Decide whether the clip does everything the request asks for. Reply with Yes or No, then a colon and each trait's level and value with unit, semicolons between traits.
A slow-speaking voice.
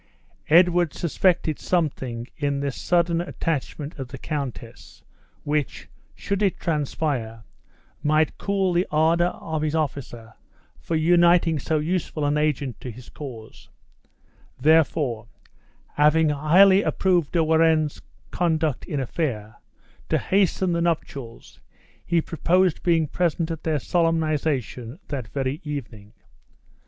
Yes: slow, 120 wpm